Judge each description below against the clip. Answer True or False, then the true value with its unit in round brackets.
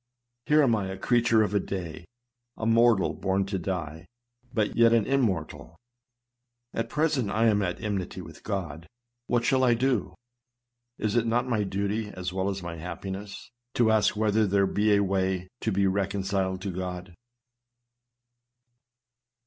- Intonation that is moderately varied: True (3.3 semitones)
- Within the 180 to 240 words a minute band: False (155 wpm)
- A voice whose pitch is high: False (100 Hz)